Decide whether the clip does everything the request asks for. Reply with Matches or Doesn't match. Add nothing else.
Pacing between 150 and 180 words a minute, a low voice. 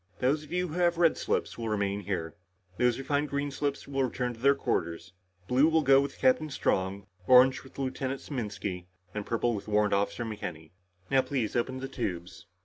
Doesn't match